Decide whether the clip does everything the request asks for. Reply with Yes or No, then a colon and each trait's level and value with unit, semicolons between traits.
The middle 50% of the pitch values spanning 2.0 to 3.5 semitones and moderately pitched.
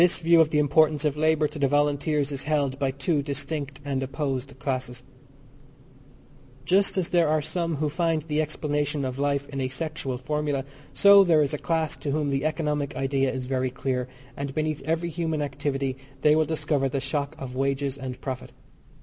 Yes: narrow, 2.4 semitones; medium, 145 Hz